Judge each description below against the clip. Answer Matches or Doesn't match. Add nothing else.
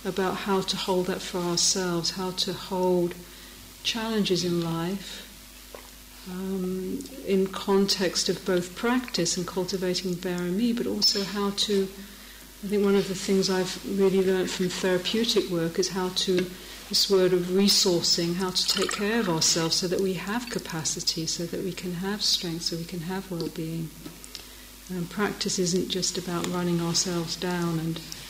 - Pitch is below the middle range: Doesn't match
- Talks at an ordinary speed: Matches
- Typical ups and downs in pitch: Doesn't match